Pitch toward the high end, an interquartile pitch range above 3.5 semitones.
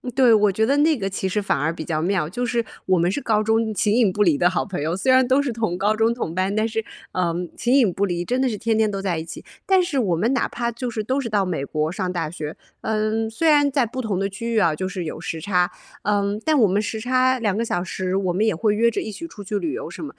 Yes: high, 210 Hz; average, 4.3 semitones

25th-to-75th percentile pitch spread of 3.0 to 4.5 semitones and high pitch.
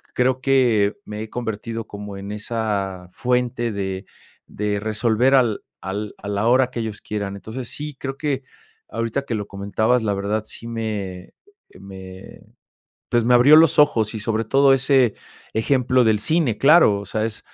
No: average, 3.6 semitones; low, 110 Hz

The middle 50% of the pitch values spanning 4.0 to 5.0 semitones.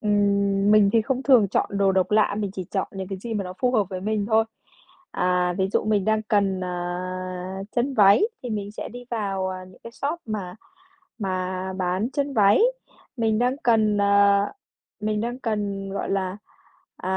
No: average, 2.7 semitones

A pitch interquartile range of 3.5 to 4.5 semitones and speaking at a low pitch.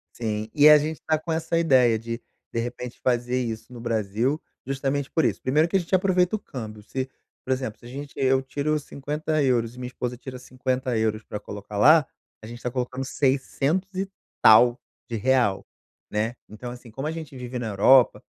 Yes: average, 3.9 semitones; low, 130 Hz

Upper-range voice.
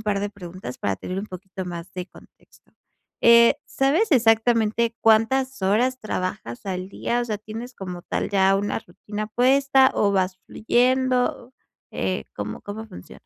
Yes: high, 215 Hz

